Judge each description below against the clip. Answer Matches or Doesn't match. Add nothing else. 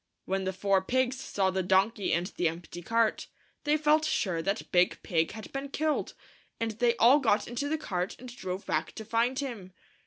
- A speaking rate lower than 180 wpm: Doesn't match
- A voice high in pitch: Matches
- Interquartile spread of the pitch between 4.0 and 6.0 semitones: Matches